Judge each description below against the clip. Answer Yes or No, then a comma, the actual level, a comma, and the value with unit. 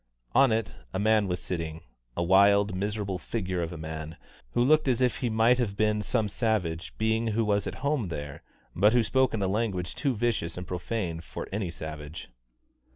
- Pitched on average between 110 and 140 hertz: No, low, 100 Hz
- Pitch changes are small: No, average, 4.5 semitones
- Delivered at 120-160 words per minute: No, average, 195 wpm